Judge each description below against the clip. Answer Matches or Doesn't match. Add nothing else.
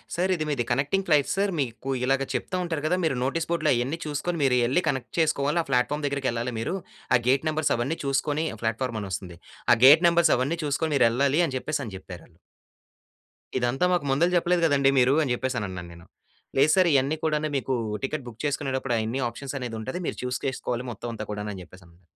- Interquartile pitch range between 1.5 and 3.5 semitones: Doesn't match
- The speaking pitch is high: Doesn't match